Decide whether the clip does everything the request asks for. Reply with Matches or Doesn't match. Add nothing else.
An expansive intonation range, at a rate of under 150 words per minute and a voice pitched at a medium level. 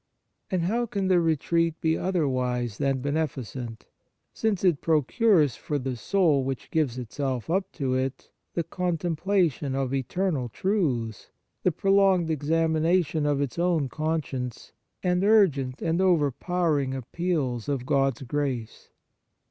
Doesn't match